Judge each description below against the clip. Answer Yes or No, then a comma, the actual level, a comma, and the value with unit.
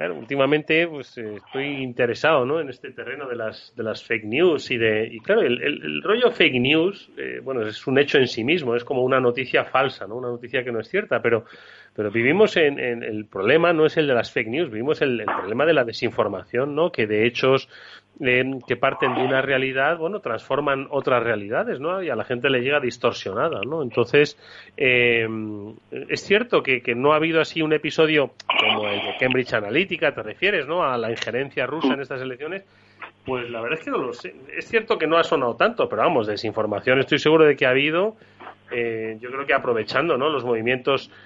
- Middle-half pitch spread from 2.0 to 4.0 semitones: No, average, 4.4 semitones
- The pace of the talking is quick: Yes, fast, 215 wpm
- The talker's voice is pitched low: Yes, low, 130 Hz